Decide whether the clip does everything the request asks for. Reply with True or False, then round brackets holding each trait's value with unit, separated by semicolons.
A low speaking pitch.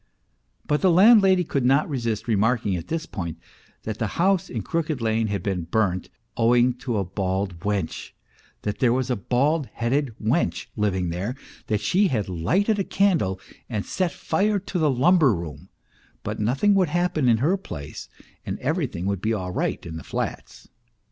True (120 Hz)